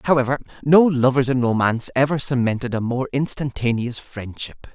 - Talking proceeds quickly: No, average, 140 wpm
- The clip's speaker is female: No, male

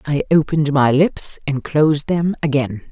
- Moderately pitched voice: Yes, medium, 145 Hz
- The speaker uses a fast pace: No, average, 165 wpm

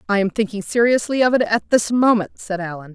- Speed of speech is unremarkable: No, fast, 225 wpm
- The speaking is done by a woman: Yes, female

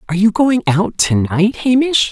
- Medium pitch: No, high, 210 Hz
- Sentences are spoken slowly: No, average, 200 wpm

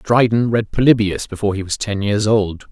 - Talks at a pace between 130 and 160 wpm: No, average, 200 wpm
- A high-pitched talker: No, low, 105 Hz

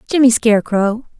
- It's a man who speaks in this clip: No, female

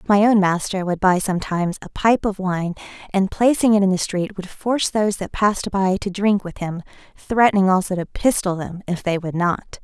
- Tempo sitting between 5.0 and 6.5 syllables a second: Yes, 5.3 syllables/s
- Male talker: No, female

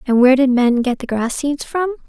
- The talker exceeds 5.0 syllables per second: Yes, 5.4 syllables/s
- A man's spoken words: No, female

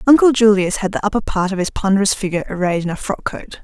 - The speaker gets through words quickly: Yes, fast, 250 wpm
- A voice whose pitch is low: No, high, 200 Hz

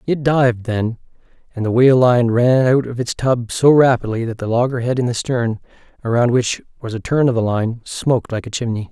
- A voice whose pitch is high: No, low, 120 Hz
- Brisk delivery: Yes, fast, 215 wpm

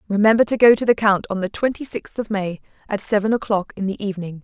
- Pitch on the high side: Yes, high, 205 Hz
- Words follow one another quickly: Yes, fast, 245 wpm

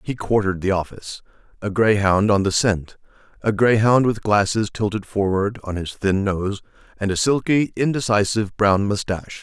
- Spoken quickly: No, average, 160 wpm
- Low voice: Yes, low, 105 Hz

